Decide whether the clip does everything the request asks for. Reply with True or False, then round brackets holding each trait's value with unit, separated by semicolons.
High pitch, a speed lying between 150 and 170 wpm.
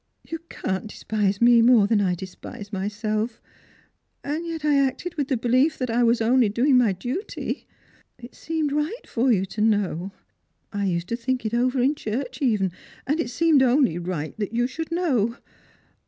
False (240 Hz; 180 wpm)